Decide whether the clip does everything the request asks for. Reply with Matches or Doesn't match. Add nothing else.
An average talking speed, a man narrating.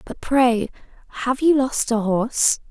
Doesn't match